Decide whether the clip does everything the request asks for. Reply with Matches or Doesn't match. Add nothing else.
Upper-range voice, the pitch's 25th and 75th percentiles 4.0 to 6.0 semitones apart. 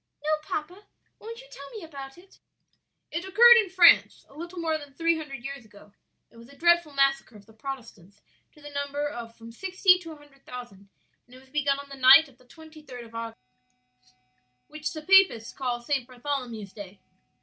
Matches